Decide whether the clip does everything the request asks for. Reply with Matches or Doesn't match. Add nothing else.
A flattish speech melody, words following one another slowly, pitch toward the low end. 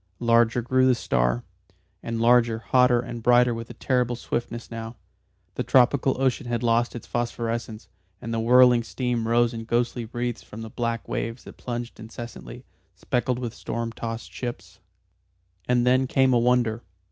Doesn't match